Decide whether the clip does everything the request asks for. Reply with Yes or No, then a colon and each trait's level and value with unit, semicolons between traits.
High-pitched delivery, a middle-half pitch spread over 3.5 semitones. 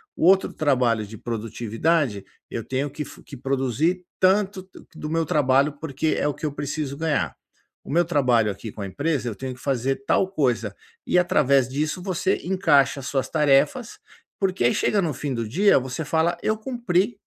No: medium, 145 Hz; average, 5.2 semitones